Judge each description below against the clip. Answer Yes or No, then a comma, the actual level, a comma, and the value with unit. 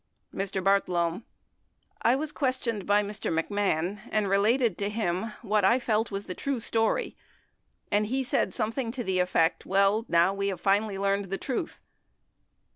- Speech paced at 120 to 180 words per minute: Yes, average, 170 wpm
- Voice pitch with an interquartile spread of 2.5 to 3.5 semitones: Yes, average, 2.8 semitones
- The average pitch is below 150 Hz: No, high, 205 Hz